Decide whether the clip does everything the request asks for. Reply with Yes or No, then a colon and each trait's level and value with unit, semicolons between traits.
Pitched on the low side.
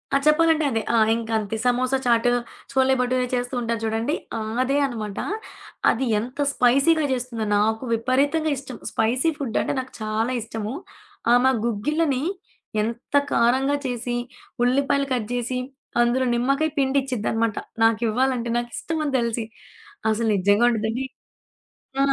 No: high, 245 Hz